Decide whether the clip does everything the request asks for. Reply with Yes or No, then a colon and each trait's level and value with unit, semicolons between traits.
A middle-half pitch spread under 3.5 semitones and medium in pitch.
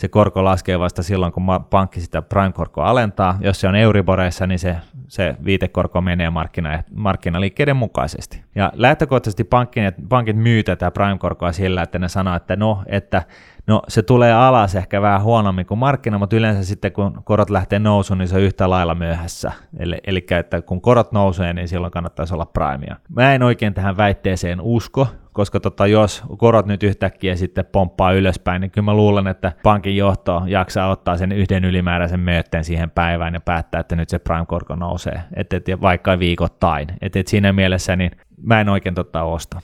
No: narrow, 2.6 semitones; very low, 95 Hz